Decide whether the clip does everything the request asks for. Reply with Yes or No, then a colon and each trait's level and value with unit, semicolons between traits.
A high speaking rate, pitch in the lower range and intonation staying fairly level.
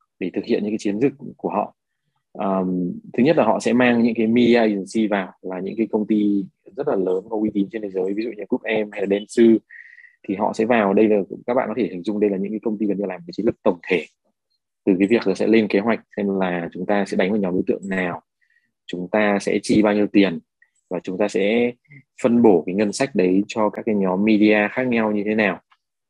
Yes: fast, 265 wpm; low, 105 Hz; narrow, 2.3 semitones